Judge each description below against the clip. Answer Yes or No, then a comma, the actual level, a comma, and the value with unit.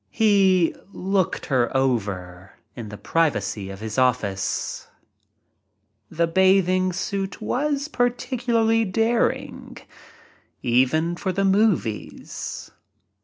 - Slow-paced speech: Yes, slow, 95 wpm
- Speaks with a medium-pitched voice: Yes, medium, 180 Hz